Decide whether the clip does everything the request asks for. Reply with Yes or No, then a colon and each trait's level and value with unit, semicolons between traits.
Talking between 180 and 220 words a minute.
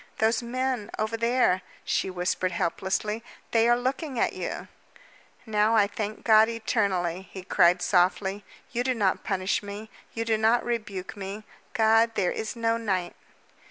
No: average, 155 wpm